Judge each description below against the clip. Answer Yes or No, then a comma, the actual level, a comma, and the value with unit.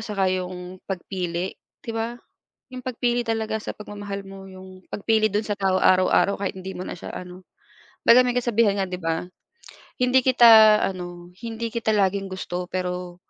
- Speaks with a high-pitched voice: Yes, high, 195 Hz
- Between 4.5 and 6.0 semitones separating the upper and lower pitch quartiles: No, average, 3.4 semitones